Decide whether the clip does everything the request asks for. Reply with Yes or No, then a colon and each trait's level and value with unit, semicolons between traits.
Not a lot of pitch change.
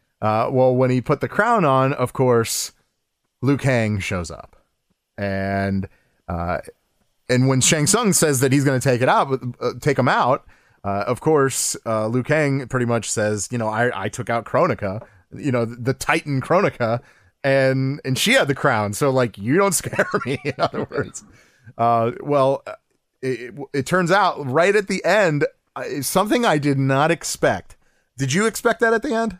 No: average, 4.2 semitones